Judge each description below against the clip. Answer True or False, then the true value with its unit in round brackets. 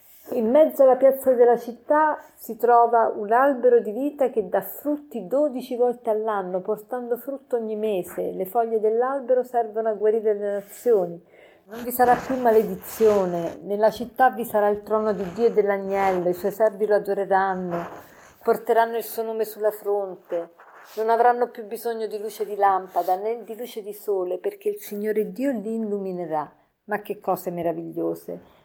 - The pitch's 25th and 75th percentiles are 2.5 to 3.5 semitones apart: True (3.2 semitones)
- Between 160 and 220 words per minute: True (165 wpm)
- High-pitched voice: True (220 Hz)